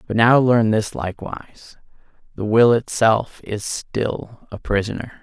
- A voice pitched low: Yes, low, 110 Hz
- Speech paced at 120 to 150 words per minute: Yes, average, 140 wpm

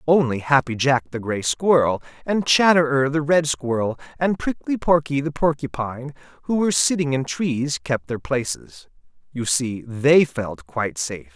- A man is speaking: Yes, male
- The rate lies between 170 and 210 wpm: No, average, 160 wpm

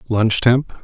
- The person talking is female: No, male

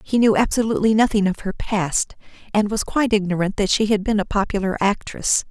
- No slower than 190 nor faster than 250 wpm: Yes, average, 195 wpm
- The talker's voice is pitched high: Yes, high, 205 Hz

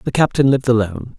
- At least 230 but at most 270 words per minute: No, fast, 205 wpm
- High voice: No, low, 125 Hz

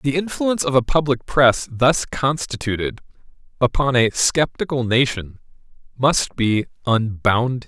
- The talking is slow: Yes, slow, 115 wpm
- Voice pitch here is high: No, low, 130 Hz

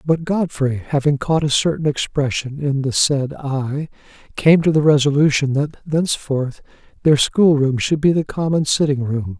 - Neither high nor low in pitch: Yes, medium, 145 Hz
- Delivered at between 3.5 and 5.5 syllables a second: Yes, 4.6 syllables/s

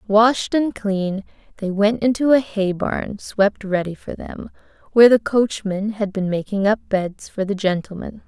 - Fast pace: No, average, 175 wpm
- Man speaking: No, female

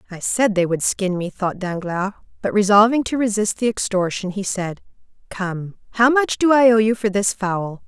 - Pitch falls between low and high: No, high, 205 Hz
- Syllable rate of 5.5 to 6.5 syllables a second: No, 4.8 syllables/s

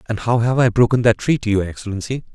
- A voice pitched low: Yes, low, 115 Hz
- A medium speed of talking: No, fast, 230 wpm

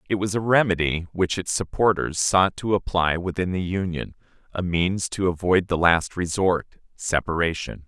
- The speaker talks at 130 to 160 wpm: Yes, average, 150 wpm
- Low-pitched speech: Yes, very low, 90 Hz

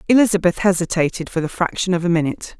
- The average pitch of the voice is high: No, medium, 180 Hz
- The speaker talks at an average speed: Yes, average, 185 wpm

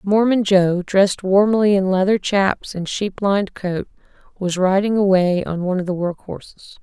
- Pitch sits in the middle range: No, high, 195 Hz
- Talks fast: No, average, 175 wpm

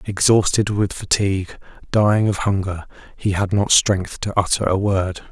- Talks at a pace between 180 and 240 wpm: No, average, 160 wpm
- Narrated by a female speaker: No, male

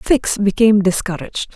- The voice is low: No, high, 205 Hz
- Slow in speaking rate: Yes, slow, 115 wpm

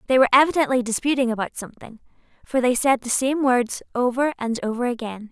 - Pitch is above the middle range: Yes, very high, 250 Hz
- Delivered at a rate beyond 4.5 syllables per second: Yes, 6.3 syllables/s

